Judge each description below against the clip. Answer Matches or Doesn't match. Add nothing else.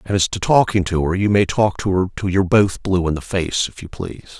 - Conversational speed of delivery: Doesn't match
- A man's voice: Matches